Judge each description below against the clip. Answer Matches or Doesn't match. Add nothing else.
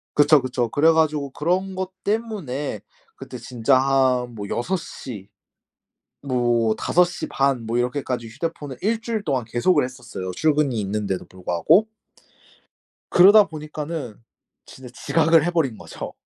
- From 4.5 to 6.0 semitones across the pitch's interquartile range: Matches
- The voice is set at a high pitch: Doesn't match